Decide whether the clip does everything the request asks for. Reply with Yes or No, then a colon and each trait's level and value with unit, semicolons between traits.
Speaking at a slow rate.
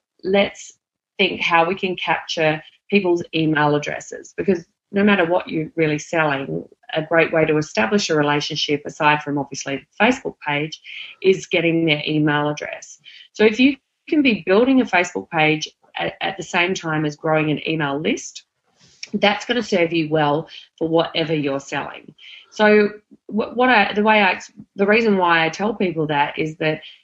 No: average, 175 wpm